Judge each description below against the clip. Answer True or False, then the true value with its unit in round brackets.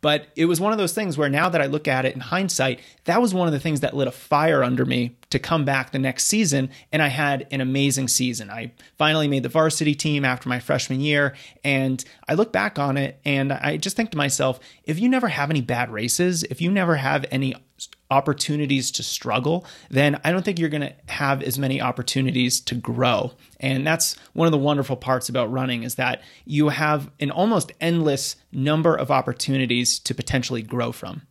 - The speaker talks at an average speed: False (215 wpm)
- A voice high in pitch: False (140 Hz)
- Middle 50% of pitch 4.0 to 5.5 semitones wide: False (3.3 semitones)